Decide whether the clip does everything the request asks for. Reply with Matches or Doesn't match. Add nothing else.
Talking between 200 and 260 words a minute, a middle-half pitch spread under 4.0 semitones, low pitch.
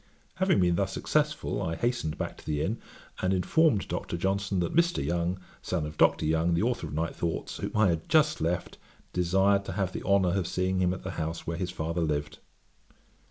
Matches